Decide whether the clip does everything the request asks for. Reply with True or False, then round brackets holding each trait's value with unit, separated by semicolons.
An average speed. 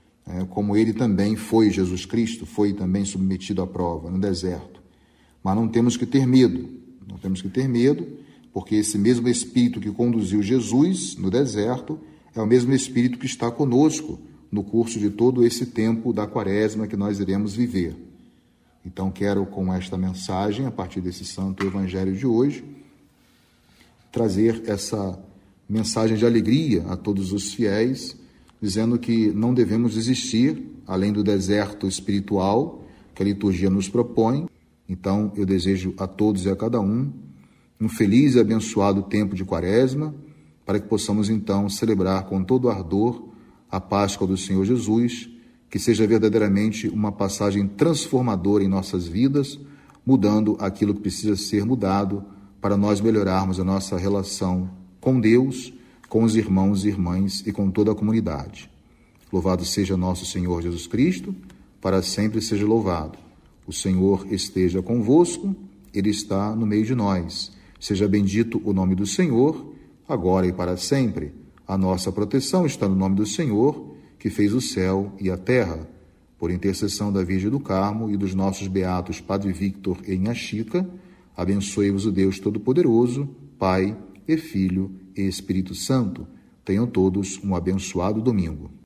True (150 wpm)